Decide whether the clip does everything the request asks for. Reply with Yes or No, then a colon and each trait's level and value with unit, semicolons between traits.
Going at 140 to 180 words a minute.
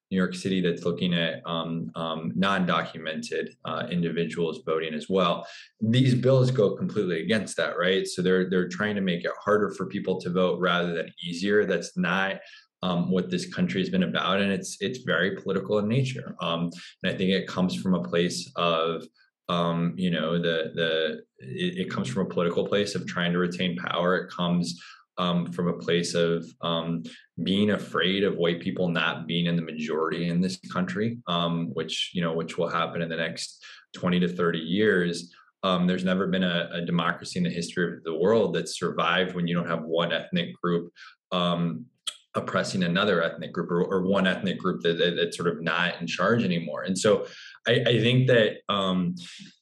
No: average, 195 wpm